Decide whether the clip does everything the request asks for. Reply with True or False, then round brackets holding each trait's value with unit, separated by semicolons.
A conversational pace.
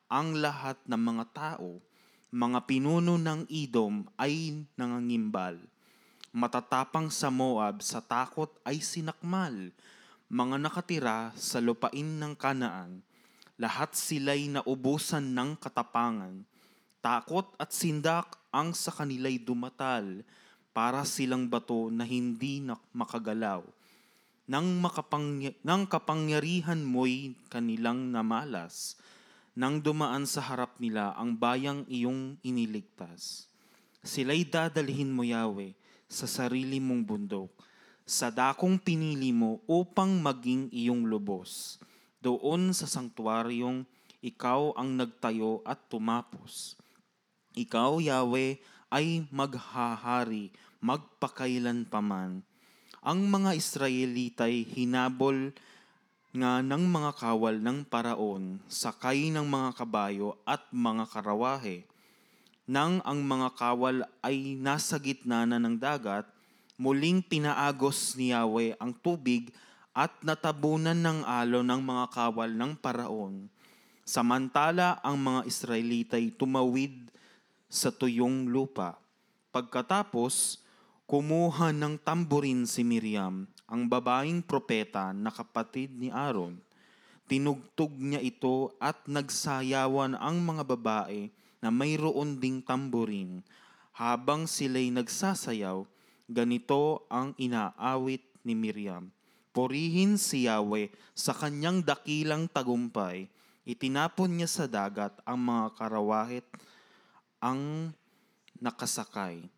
False (100 wpm)